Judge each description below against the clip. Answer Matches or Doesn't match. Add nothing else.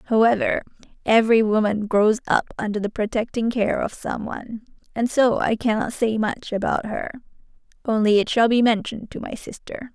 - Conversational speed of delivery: Matches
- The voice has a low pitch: Doesn't match